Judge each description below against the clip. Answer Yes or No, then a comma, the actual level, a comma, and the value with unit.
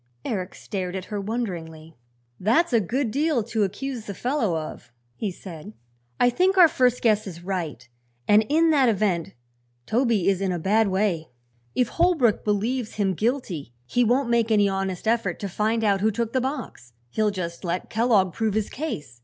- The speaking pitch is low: No, high, 210 Hz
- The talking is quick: No, average, 180 wpm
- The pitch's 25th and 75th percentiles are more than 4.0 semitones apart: Yes, average, 4.6 semitones